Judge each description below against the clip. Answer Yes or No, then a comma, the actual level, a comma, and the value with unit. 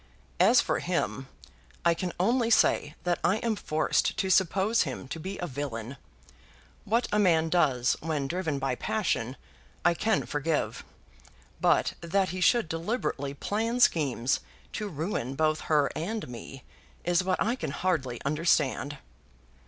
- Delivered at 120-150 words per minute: Yes, average, 145 wpm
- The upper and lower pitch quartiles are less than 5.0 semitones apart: No, wide, 5.4 semitones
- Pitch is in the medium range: Yes, medium, 165 Hz